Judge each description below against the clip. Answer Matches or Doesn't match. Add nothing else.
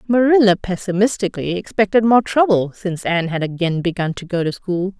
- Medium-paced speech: Matches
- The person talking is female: Matches